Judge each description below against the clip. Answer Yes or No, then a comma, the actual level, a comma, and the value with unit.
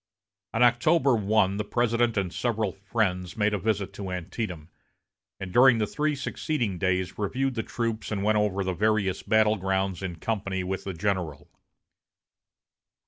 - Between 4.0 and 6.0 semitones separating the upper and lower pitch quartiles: No, average, 3.1 semitones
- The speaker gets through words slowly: No, average, 155 wpm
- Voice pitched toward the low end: Yes, low, 105 Hz